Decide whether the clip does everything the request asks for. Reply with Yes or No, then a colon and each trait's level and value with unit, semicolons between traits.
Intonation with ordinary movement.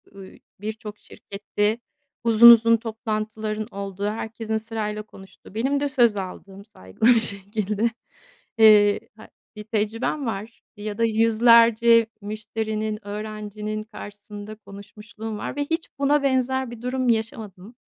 No: narrow, 1.8 semitones